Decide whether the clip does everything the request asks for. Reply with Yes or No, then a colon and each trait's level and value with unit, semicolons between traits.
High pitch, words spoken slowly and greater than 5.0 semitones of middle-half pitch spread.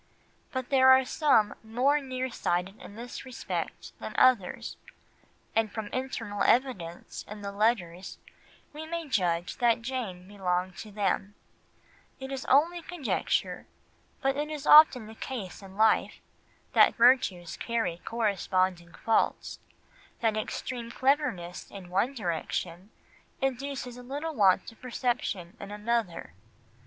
Yes: high, 225 Hz; slow, 130 wpm; wide, 5.4 semitones